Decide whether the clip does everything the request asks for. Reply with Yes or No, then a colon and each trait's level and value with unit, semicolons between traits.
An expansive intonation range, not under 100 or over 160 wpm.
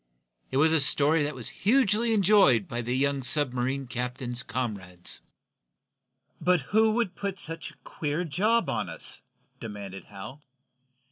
Yes: wide, 7.1 semitones; average, 145 wpm